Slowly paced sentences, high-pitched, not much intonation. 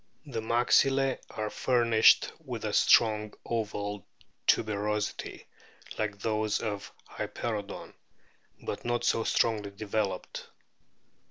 No: slow, 95 wpm; low, 110 Hz; narrow, 2.1 semitones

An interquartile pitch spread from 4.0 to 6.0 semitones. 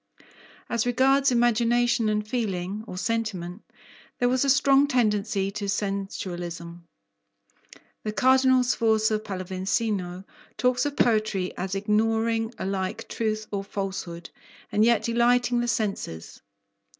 No: average, 3.6 semitones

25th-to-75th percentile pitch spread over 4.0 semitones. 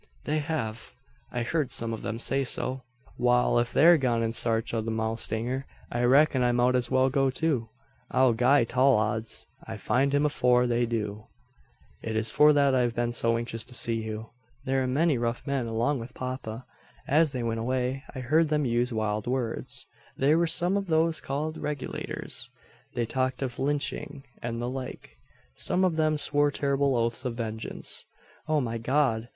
No: average, 3.4 semitones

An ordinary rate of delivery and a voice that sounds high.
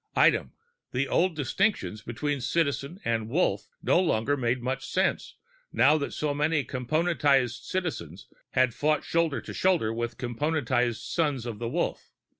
No: average, 145 wpm; low, 135 Hz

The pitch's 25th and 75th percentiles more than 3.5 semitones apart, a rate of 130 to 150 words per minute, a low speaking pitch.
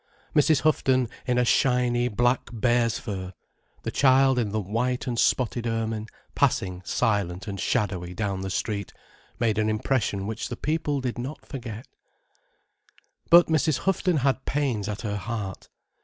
Yes: average, 4.1 semitones; average, 145 wpm; low, 120 Hz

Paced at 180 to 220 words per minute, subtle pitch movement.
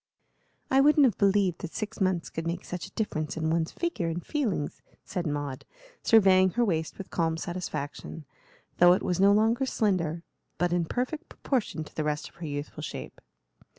No: average, 185 wpm; average, 4.7 semitones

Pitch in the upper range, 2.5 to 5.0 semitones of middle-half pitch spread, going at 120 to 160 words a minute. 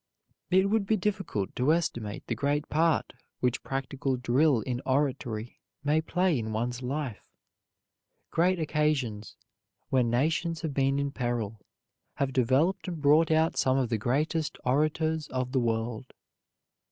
No: medium, 140 Hz; average, 4.4 semitones; average, 140 wpm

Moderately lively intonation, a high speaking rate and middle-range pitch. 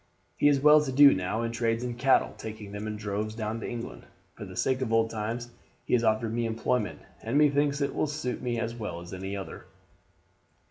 No: average, 3.1 semitones; fast, 220 wpm; low, 115 Hz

